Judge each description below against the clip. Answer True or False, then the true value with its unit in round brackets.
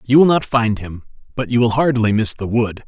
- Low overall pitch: True (115 Hz)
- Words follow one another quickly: True (250 wpm)